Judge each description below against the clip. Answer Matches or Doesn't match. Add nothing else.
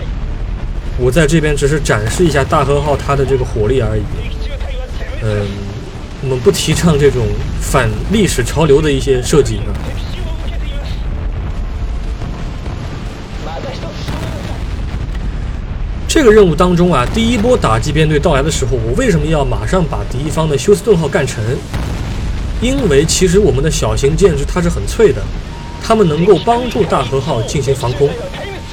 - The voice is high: Doesn't match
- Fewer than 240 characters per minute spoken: Matches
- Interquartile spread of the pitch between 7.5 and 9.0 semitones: Doesn't match